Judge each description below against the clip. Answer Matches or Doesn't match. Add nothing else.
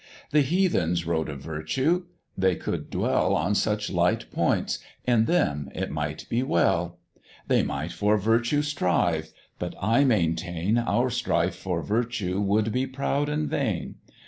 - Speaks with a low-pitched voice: Matches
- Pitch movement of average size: Doesn't match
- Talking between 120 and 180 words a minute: Matches